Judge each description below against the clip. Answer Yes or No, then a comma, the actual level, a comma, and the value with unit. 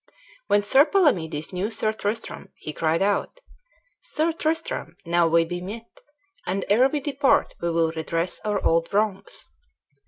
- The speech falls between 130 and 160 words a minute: Yes, average, 150 wpm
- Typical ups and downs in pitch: No, wide, 7.4 semitones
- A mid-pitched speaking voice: No, high, 200 Hz